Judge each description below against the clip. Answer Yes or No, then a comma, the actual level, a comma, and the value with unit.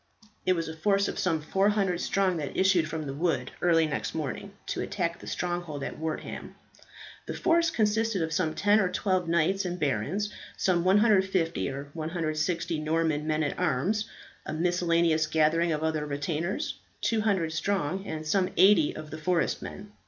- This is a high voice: No, medium, 170 Hz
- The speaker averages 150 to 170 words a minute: Yes, average, 165 wpm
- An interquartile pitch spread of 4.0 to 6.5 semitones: No, average, 3.6 semitones